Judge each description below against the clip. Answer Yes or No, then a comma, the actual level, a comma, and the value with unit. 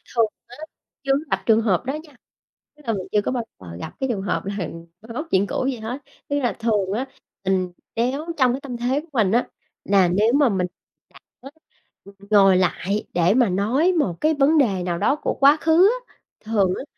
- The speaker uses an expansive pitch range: Yes, wide, 5.8 semitones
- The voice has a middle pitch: No, high, 230 Hz